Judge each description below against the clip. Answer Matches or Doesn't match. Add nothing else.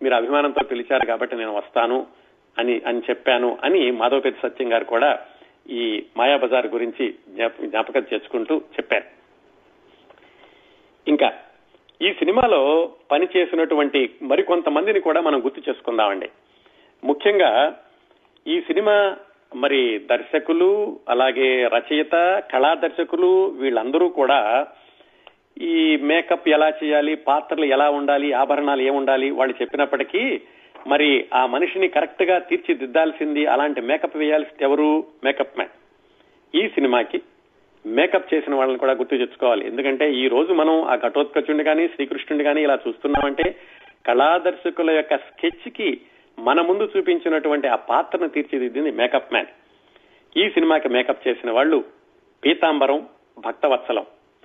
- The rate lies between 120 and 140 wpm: Doesn't match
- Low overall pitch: Doesn't match